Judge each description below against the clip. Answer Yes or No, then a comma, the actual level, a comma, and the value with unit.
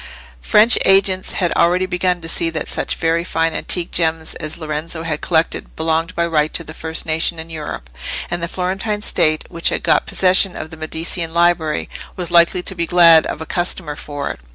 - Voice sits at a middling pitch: Yes, medium, 165 Hz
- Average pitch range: No, narrow, 1.9 semitones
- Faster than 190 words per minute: Yes, average, 200 wpm